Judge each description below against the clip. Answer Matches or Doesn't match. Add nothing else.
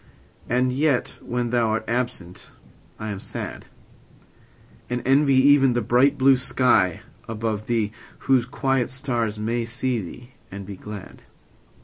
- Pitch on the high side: Doesn't match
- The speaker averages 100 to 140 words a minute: Matches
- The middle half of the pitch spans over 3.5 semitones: Doesn't match